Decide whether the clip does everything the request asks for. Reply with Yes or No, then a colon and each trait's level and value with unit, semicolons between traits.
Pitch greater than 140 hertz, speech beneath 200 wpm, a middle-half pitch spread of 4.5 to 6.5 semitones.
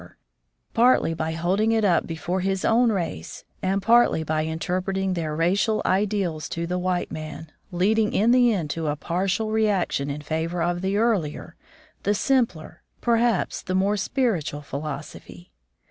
Yes: medium, 185 Hz; average, 160 wpm; average, 4.8 semitones